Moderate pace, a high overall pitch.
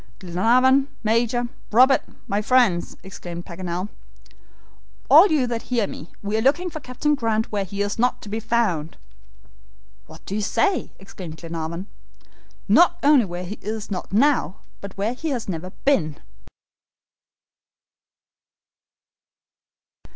No: slow, 130 wpm; high, 215 Hz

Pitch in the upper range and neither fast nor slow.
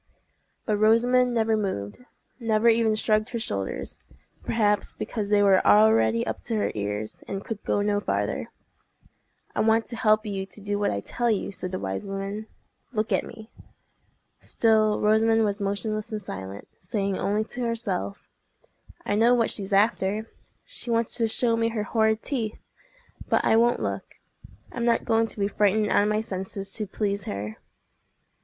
Yes: high, 215 Hz; average, 165 wpm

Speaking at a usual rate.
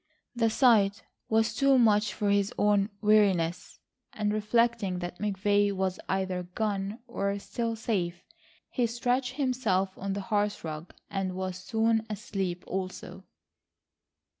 No: slow, 130 wpm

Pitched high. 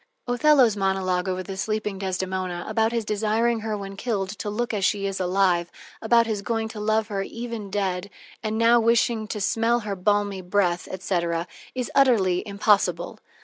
Yes: high, 205 Hz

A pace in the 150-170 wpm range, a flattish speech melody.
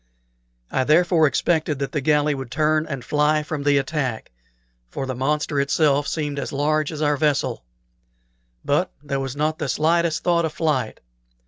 Yes: average, 165 wpm; narrow, 2.0 semitones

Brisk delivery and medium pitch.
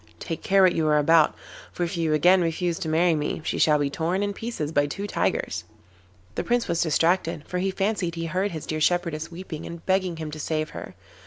Yes: fast, 225 wpm; medium, 165 Hz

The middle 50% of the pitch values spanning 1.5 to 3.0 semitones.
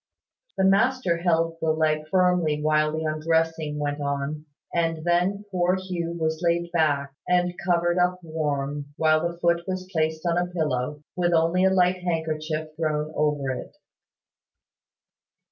Yes: narrow, 2.4 semitones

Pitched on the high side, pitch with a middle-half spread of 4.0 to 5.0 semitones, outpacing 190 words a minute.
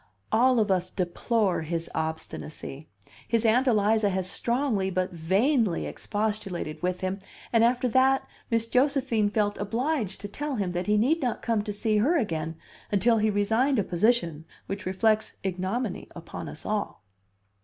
No: high, 210 Hz; average, 4.3 semitones; average, 155 wpm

